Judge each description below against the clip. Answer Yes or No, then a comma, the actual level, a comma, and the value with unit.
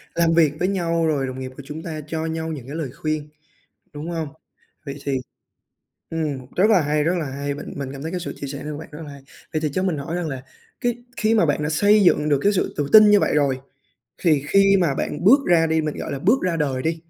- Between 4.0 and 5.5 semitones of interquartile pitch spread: No, average, 3.3 semitones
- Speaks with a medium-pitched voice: Yes, medium, 155 Hz